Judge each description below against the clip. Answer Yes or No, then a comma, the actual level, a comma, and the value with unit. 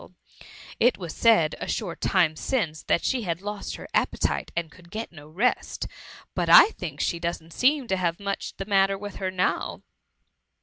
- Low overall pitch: No, medium, 185 Hz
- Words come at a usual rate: Yes, average, 185 wpm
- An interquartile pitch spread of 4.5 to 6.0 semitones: No, average, 4.0 semitones